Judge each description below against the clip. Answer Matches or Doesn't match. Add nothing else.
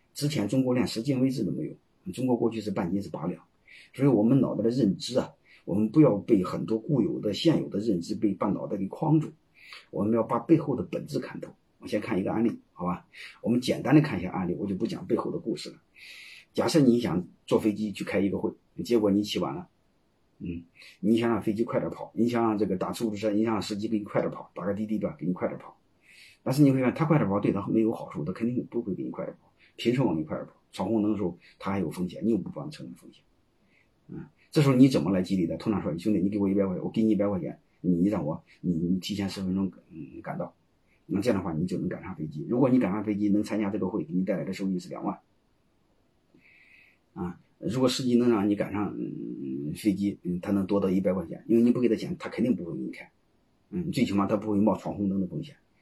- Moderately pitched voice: Doesn't match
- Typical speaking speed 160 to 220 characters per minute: Doesn't match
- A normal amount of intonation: Matches